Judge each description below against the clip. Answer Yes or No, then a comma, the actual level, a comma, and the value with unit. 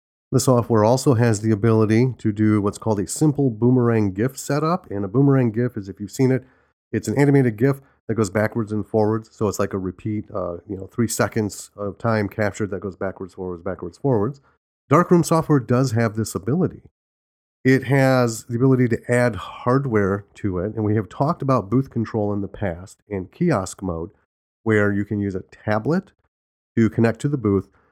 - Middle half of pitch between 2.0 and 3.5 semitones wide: No, average, 4.3 semitones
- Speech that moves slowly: No, average, 195 wpm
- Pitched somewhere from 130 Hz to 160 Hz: No, low, 110 Hz